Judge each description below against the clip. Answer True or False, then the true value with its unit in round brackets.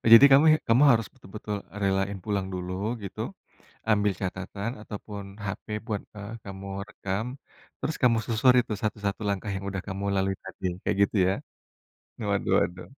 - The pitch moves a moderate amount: False (2.2 semitones)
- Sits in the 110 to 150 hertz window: False (100 Hz)